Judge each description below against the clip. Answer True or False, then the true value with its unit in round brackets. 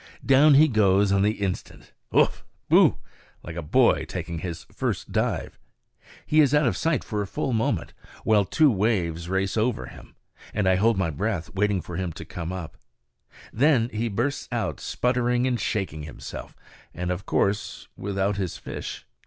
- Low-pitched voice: True (100 Hz)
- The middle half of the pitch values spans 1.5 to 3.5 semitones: False (4.4 semitones)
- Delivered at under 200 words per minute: True (170 wpm)